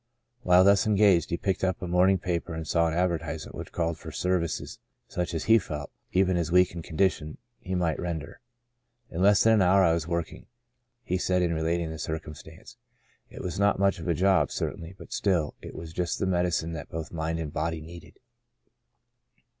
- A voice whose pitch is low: Yes, very low, 85 Hz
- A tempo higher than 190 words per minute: Yes, fast, 205 wpm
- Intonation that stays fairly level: Yes, narrow, 2.2 semitones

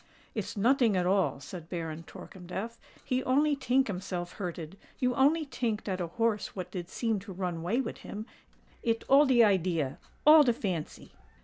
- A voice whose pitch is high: Yes, high, 205 Hz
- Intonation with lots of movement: Yes, wide, 5.9 semitones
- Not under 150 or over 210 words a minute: Yes, average, 155 wpm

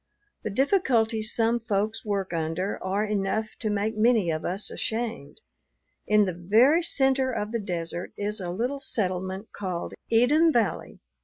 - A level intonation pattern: No, average, 3.8 semitones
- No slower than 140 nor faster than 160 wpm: Yes, average, 150 wpm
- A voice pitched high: Yes, high, 215 Hz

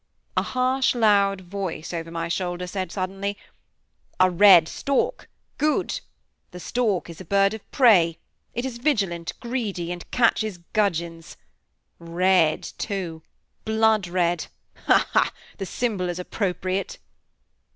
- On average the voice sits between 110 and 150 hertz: No, high, 190 Hz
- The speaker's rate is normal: No, slow, 125 wpm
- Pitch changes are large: No, average, 4.0 semitones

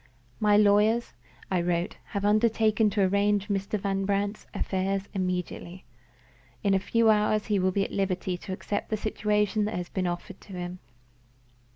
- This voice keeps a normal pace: Yes, average, 165 wpm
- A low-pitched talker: No, high, 200 Hz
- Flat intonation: Yes, narrow, 2.0 semitones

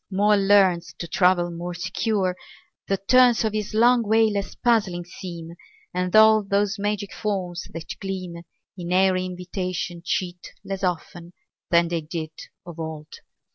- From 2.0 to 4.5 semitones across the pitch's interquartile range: Yes, average, 2.8 semitones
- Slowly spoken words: No, average, 145 wpm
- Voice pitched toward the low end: No, medium, 185 Hz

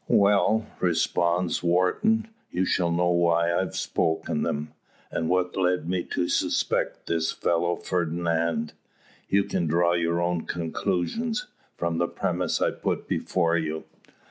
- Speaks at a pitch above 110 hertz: No, very low, 85 Hz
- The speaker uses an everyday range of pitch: No, narrow, 1.5 semitones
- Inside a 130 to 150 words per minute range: Yes, slow, 135 wpm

